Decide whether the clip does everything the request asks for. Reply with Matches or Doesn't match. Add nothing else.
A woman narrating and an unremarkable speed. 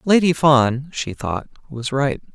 Doesn't match